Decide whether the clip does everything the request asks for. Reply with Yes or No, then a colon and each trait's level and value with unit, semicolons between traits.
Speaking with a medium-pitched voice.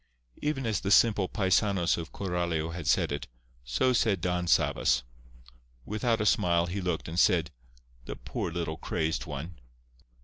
No: very low, 90 Hz